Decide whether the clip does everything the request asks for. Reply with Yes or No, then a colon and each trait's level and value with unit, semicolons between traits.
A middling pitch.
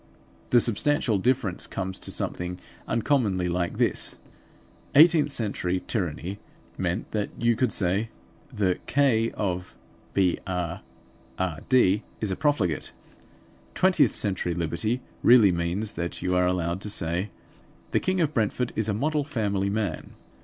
No: low, 100 Hz